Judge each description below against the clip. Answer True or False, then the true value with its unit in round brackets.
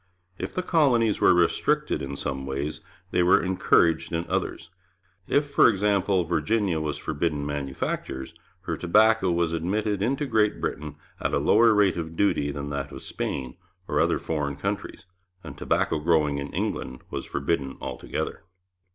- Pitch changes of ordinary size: False (6.0 semitones)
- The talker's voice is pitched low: True (85 Hz)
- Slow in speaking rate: False (155 wpm)